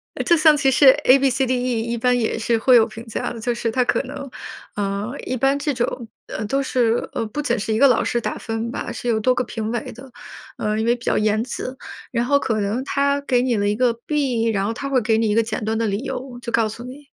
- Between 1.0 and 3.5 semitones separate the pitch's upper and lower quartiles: Yes, average, 2.8 semitones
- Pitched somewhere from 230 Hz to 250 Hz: Yes, high, 240 Hz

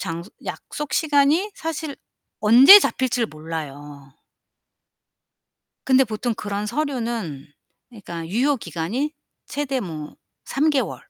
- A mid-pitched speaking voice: No, high, 230 Hz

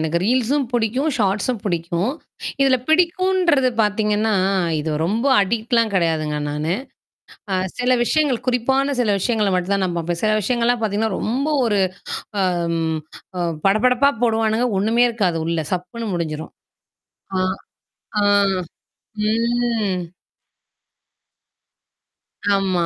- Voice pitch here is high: Yes, high, 220 Hz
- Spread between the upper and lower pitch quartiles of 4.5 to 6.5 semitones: Yes, average, 5.1 semitones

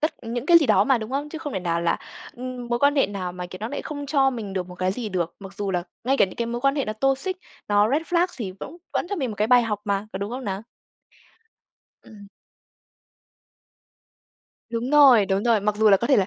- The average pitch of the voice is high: Yes, high, 230 Hz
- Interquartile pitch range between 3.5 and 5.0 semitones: No, wide, 5.4 semitones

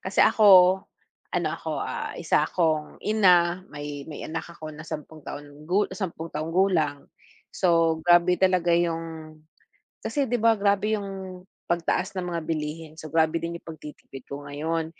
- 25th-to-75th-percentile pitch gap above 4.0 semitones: No, average, 3.0 semitones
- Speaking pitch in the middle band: Yes, medium, 165 Hz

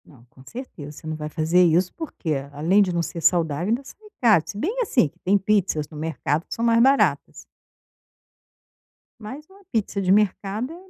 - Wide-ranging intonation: Yes, wide, 6.4 semitones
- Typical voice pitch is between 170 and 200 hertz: Yes, high, 190 Hz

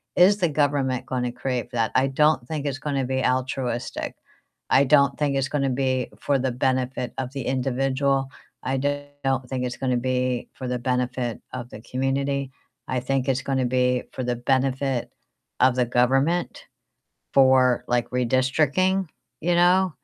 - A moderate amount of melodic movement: No, narrow, 1.6 semitones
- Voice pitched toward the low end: Yes, low, 130 Hz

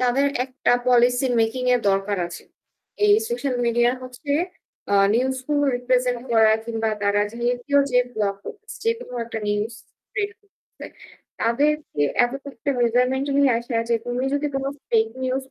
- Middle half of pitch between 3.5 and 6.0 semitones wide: No, average, 2.9 semitones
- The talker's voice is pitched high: Yes, high, 245 Hz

